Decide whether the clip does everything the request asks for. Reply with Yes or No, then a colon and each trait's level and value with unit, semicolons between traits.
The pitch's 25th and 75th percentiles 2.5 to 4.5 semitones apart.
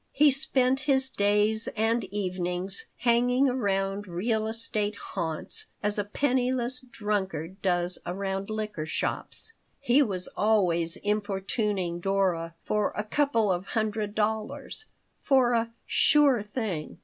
Yes: average, 3.9 semitones